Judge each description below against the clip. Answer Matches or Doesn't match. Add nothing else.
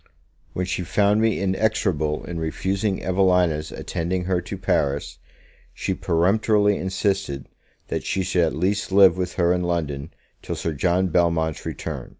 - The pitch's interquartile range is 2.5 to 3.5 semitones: Matches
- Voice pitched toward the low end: Matches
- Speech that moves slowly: Doesn't match